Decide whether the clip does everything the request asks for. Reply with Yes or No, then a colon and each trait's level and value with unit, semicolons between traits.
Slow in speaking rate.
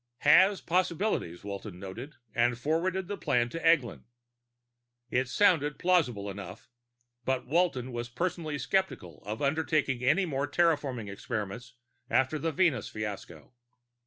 Yes: slow, 130 wpm